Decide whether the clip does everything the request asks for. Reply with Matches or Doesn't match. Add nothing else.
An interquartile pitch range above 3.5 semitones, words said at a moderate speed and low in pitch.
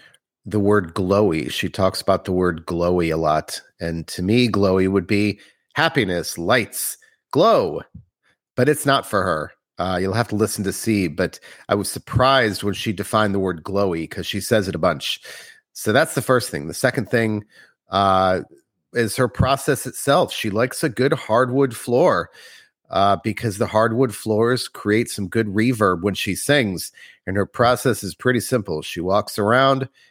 Matches